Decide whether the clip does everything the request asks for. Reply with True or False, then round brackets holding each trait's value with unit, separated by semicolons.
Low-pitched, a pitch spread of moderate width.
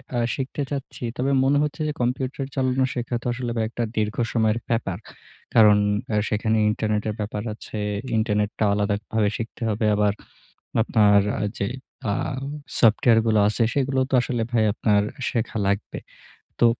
True (110 Hz; 3.1 semitones)